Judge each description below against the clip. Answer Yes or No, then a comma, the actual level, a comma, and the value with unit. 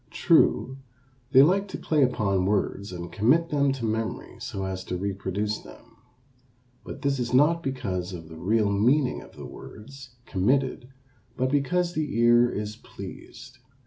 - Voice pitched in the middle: No, low, 120 Hz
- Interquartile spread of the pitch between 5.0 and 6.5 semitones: Yes, wide, 5.5 semitones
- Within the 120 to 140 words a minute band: No, average, 155 wpm